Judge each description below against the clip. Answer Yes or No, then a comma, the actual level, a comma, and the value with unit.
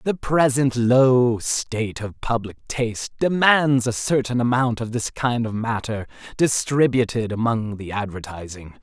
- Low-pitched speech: Yes, low, 120 Hz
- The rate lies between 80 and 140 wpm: Yes, slow, 135 wpm